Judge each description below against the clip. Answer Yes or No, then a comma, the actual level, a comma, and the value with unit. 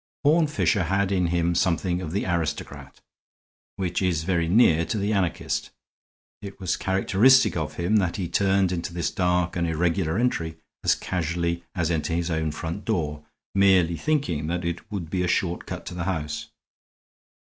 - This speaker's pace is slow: No, average, 170 wpm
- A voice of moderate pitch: No, very low, 90 Hz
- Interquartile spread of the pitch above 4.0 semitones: No, average, 2.7 semitones